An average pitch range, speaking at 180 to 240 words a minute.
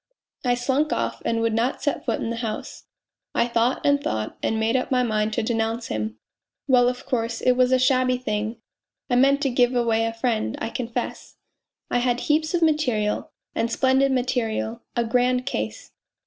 No: narrow, 2.1 semitones; average, 190 wpm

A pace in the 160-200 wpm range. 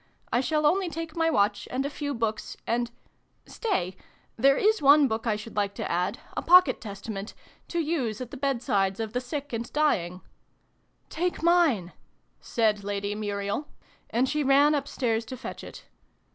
Yes: average, 175 wpm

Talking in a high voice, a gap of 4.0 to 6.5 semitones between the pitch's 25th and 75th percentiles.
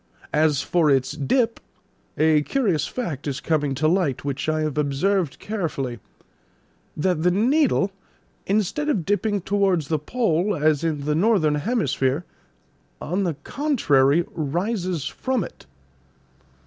No: medium, 165 Hz; wide, 5.5 semitones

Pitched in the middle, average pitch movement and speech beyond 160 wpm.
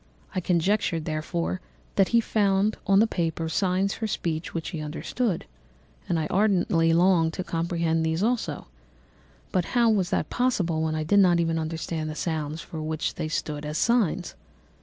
Yes: medium, 170 Hz; average, 3.5 semitones; average, 170 wpm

